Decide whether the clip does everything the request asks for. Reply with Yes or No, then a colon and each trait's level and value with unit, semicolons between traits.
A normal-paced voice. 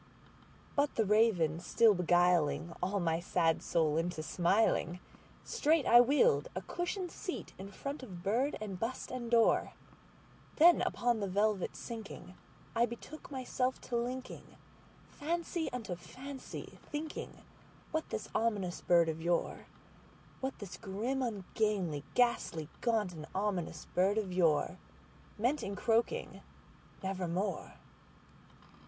No: slow, 110 wpm